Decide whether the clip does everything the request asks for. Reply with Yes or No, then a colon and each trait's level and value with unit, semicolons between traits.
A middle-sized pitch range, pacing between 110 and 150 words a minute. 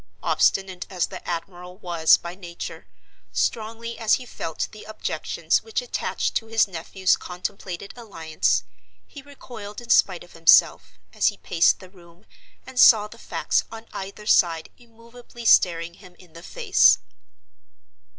Yes: average, 4.6 semitones; average, 145 wpm